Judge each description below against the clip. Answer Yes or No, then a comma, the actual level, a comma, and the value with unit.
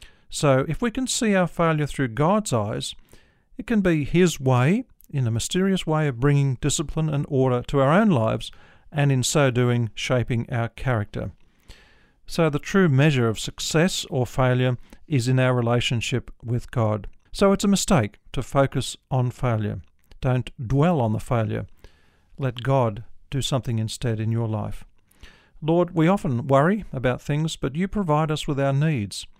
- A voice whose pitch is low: Yes, low, 130 Hz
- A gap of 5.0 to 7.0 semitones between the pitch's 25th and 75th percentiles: Yes, wide, 5.4 semitones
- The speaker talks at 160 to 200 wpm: Yes, average, 170 wpm